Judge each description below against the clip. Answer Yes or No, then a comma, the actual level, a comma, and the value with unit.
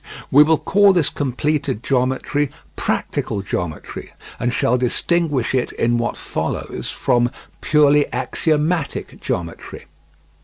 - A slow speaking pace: Yes, slow, 110 wpm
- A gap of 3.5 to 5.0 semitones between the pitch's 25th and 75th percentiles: Yes, average, 3.8 semitones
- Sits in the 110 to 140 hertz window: Yes, low, 135 Hz